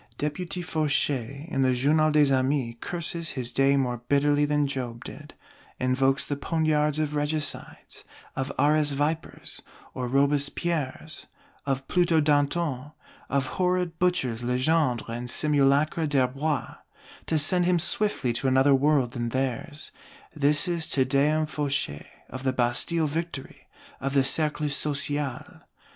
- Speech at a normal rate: No, slow, 130 wpm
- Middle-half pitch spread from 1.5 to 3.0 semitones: Yes, average, 2.7 semitones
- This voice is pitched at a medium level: Yes, medium, 145 Hz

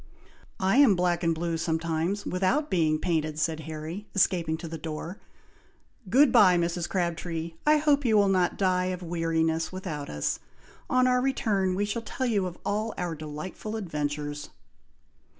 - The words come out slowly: No, average, 155 wpm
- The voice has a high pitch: No, medium, 175 Hz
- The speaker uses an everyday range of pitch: Yes, average, 4.1 semitones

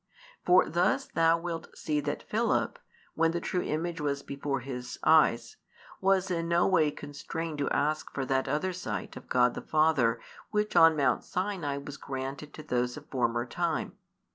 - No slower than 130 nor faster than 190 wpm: Yes, average, 170 wpm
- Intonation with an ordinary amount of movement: Yes, average, 3.7 semitones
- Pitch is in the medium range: Yes, medium, 155 Hz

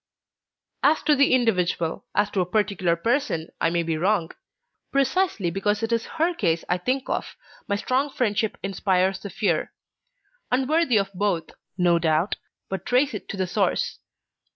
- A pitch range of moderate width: No, wide, 6.1 semitones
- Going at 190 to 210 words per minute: No, average, 160 wpm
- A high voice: Yes, high, 200 Hz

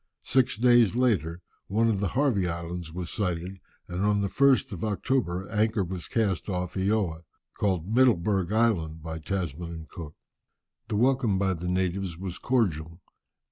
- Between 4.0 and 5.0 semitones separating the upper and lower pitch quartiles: Yes, average, 4.3 semitones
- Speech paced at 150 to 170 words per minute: Yes, average, 155 wpm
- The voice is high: No, very low, 95 Hz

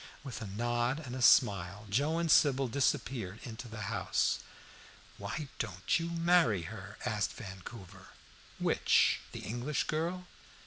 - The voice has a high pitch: No, low, 120 Hz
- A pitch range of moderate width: No, wide, 6.2 semitones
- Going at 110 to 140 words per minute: Yes, slow, 135 wpm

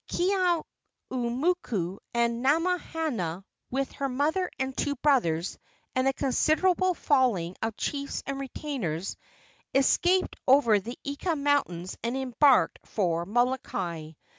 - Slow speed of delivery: Yes, slow, 110 wpm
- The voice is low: No, very high, 265 Hz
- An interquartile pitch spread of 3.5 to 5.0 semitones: No, wide, 5.6 semitones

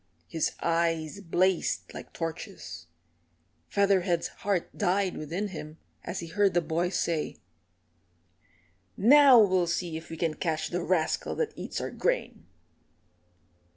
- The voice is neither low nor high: Yes, medium, 175 Hz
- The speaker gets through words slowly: Yes, slow, 125 wpm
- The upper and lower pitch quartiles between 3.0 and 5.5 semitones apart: Yes, average, 3.3 semitones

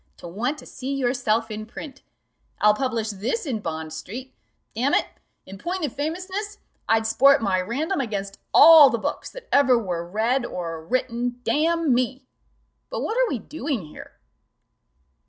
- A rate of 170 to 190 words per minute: No, average, 160 wpm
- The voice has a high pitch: Yes, high, 245 Hz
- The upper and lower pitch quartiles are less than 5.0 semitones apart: No, average, 5.3 semitones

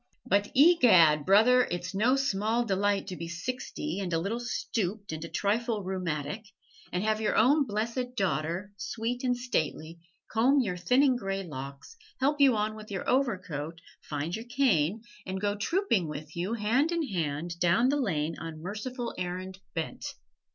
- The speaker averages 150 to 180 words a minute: Yes, average, 165 wpm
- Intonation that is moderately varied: No, wide, 6.0 semitones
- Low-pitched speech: No, high, 205 Hz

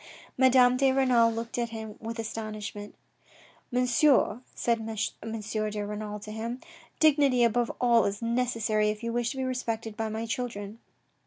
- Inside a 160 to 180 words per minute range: Yes, average, 165 wpm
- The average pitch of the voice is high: Yes, high, 230 Hz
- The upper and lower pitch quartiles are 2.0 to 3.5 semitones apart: Yes, narrow, 2.4 semitones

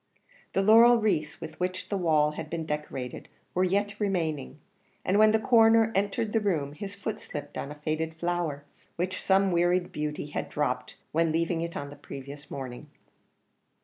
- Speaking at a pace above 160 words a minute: Yes, average, 175 wpm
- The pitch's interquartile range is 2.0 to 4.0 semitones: No, average, 5.0 semitones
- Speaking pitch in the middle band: Yes, medium, 170 Hz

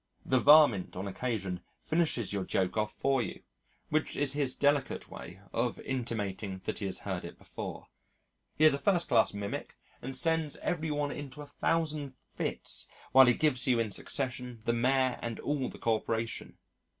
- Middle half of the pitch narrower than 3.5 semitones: No, average, 5.2 semitones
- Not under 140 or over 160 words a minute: No, average, 175 wpm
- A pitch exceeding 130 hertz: No, low, 125 Hz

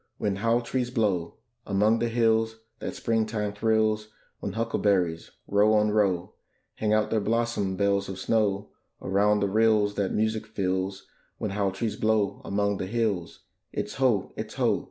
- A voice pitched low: Yes, low, 105 Hz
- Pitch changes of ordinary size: No, narrow, 2.0 semitones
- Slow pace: No, average, 155 wpm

